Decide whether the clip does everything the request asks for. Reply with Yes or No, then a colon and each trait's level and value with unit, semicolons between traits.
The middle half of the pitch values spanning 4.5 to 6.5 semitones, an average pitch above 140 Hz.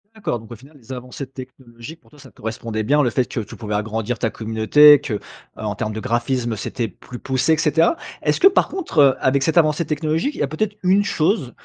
No: average, 5.1 semitones; low, 130 Hz